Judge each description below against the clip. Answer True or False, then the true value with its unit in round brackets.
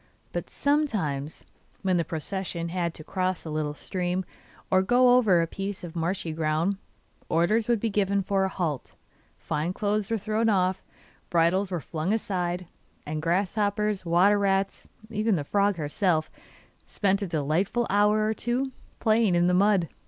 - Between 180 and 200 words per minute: False (160 wpm)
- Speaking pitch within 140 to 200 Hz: True (190 Hz)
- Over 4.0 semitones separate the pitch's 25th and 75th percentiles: False (3.5 semitones)